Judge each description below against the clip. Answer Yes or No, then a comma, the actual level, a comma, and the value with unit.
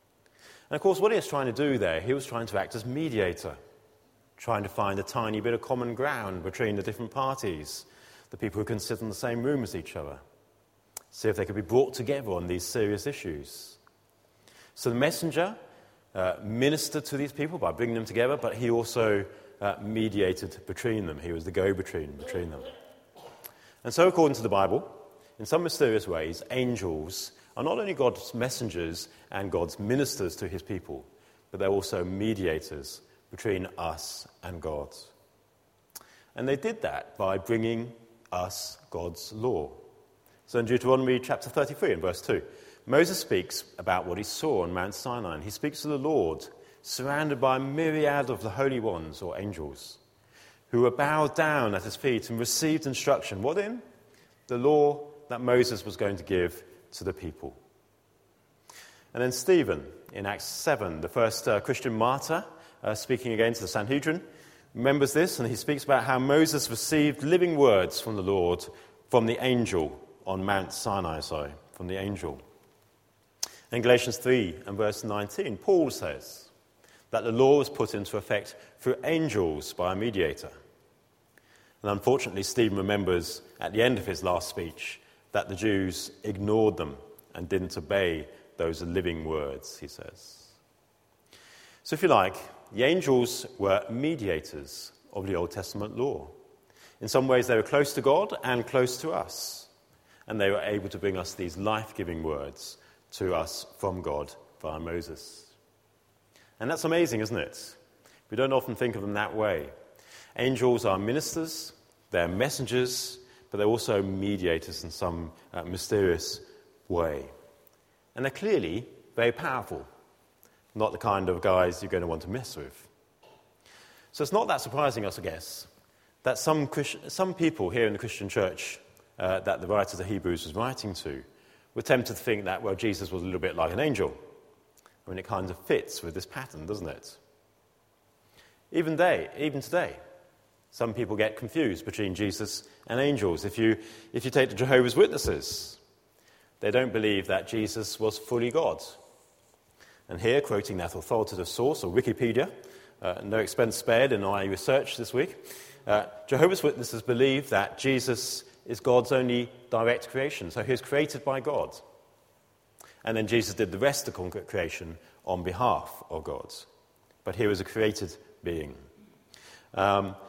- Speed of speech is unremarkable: Yes, average, 170 wpm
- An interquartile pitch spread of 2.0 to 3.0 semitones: No, wide, 5.6 semitones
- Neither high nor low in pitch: No, low, 115 Hz